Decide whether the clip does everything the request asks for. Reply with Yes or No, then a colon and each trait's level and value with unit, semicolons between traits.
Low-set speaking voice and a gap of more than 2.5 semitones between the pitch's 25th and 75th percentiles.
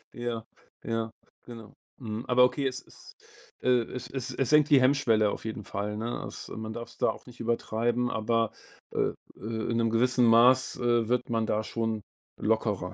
No: low, 115 Hz; narrow, 1.9 semitones